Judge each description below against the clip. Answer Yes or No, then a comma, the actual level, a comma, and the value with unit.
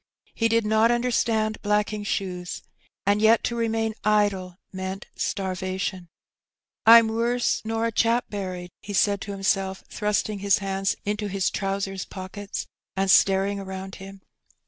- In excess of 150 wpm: No, average, 145 wpm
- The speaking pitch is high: Yes, high, 200 Hz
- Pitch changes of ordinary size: No, narrow, 2.3 semitones